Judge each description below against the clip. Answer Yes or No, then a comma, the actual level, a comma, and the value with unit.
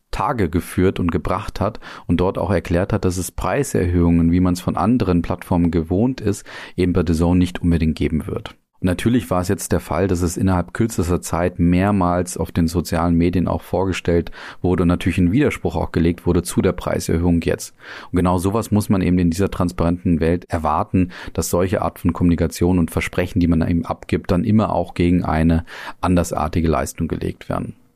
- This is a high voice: No, very low, 90 Hz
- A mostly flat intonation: Yes, narrow, 1.5 semitones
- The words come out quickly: Yes, fast, 195 wpm